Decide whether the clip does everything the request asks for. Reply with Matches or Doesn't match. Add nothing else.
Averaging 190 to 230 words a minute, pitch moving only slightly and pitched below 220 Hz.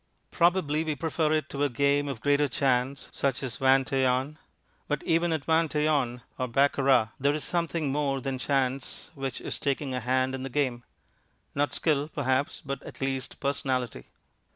Doesn't match